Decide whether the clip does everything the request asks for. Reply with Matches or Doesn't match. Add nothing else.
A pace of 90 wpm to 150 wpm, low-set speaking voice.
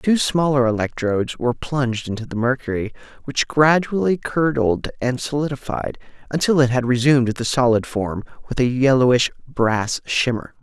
Matches